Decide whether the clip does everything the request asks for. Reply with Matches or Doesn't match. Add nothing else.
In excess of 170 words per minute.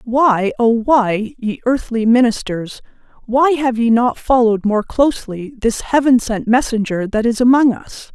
Doesn't match